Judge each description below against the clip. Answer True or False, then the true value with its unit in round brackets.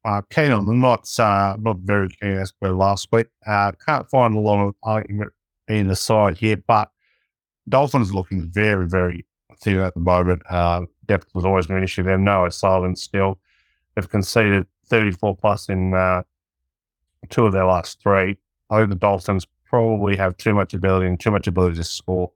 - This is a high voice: False (100 Hz)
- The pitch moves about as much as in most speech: False (2.3 semitones)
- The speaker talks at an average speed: True (190 wpm)